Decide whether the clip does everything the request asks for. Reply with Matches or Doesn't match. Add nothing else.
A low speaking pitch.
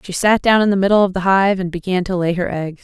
Doesn't match